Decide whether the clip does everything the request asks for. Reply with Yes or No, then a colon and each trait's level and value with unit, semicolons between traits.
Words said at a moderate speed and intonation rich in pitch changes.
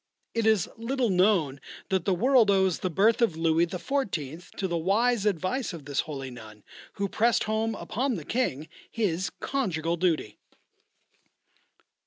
Yes: average, 150 wpm; wide, 5.7 semitones